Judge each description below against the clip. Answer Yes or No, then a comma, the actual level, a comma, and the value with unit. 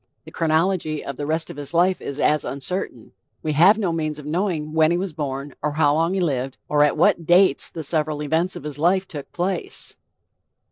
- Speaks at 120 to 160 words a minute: No, fast, 205 wpm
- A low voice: No, medium, 155 Hz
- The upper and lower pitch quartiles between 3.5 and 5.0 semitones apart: No, average, 3.0 semitones